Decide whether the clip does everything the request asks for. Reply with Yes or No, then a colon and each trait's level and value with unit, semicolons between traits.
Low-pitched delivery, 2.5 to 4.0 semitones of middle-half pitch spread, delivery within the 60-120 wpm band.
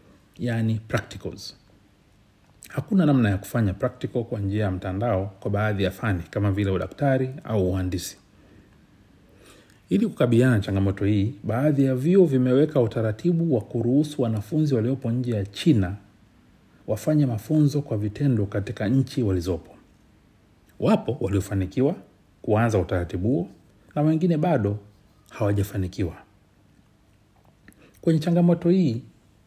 No: low, 105 Hz; average, 4.6 semitones; average, 110 wpm